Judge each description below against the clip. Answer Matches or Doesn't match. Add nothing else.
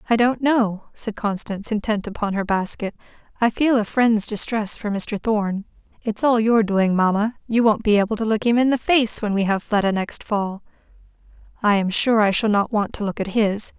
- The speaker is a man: Doesn't match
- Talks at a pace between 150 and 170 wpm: Doesn't match